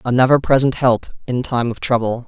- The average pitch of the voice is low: Yes, low, 125 Hz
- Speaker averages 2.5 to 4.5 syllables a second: No, 5.5 syllables/s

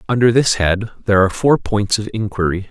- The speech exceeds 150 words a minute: Yes, average, 200 wpm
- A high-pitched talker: No, low, 105 Hz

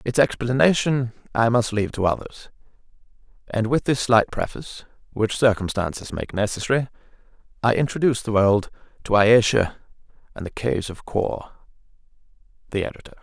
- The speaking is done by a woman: No, male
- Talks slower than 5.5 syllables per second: No, 5.6 syllables/s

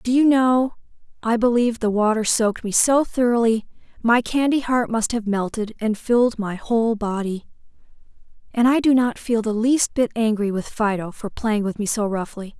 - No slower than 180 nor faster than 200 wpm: Yes, average, 185 wpm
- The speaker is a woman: Yes, female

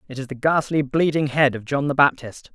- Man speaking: Yes, male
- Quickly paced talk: Yes, fast, 235 wpm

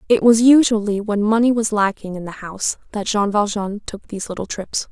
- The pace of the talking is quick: Yes, fast, 210 wpm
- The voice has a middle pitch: No, high, 210 Hz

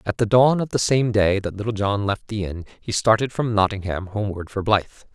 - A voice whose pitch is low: Yes, low, 105 Hz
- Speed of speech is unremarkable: No, fast, 235 wpm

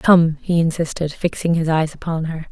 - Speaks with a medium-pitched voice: Yes, medium, 165 Hz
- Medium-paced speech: Yes, average, 190 wpm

